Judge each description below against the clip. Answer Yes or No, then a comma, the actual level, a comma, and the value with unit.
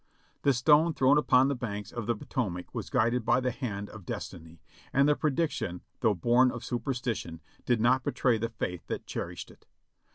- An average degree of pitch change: Yes, average, 3.9 semitones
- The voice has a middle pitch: No, low, 120 Hz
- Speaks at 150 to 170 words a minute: No, average, 190 wpm